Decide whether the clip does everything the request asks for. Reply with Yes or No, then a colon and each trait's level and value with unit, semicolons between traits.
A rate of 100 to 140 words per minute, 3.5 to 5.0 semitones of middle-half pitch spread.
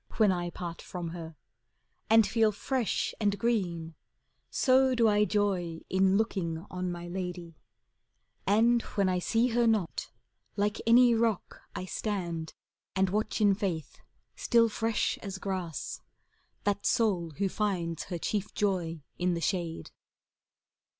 Yes: slow, 135 wpm; average, 4.0 semitones